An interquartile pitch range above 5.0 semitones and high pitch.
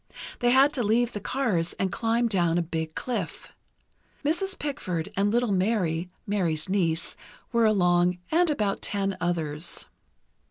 Yes: wide, 5.5 semitones; high, 200 Hz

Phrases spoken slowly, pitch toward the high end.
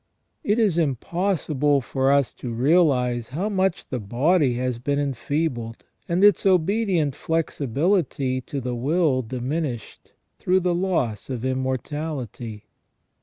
No: slow, 120 wpm; medium, 140 Hz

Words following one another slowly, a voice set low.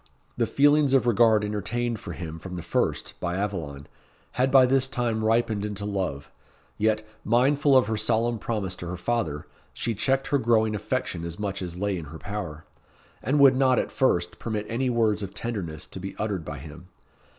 No: average, 190 wpm; low, 105 Hz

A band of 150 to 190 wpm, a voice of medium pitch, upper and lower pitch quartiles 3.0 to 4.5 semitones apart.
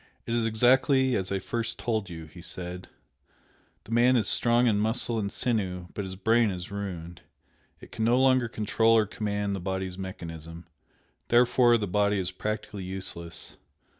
No: average, 170 wpm; low, 105 Hz; average, 3.9 semitones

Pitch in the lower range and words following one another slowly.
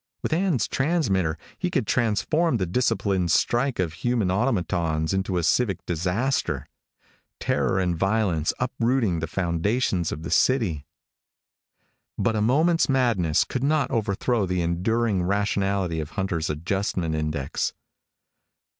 Yes: very low, 95 Hz; slow, 125 wpm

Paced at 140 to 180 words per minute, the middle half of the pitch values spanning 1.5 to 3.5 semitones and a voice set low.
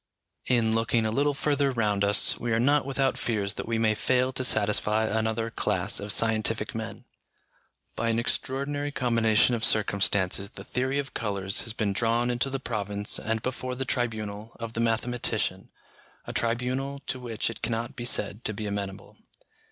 Yes: average, 175 wpm; average, 2.8 semitones; low, 115 Hz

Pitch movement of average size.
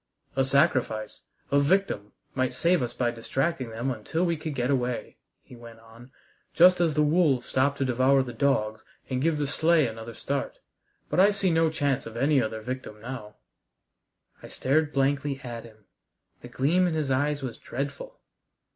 Yes: average, 4.2 semitones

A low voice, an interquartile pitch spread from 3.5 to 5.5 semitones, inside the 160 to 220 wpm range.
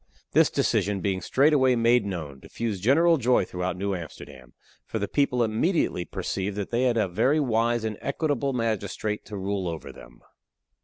Yes: low, 110 Hz; average, 5.0 semitones; average, 165 wpm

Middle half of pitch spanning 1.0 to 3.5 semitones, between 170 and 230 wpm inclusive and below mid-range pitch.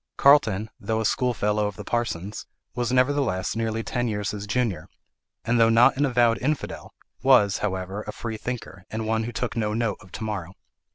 Yes: average, 2.8 semitones; average, 180 wpm; low, 110 Hz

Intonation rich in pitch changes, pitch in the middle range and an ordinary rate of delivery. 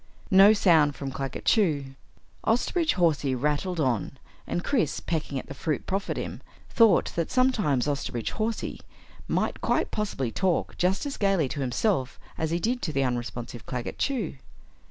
Yes: wide, 6.9 semitones; medium, 160 Hz; average, 155 wpm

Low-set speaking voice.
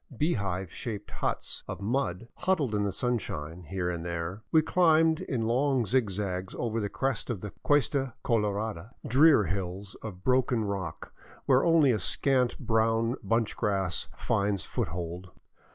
Yes: low, 110 Hz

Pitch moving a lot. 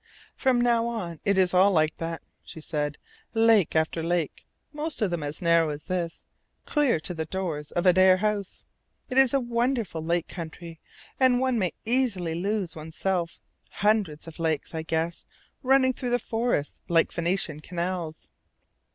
Yes: wide, 5.7 semitones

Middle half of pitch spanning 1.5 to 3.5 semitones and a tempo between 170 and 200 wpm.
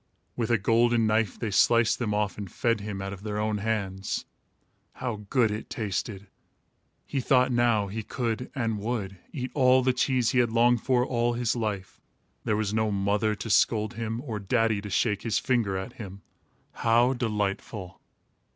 Yes: narrow, 2.6 semitones; average, 180 wpm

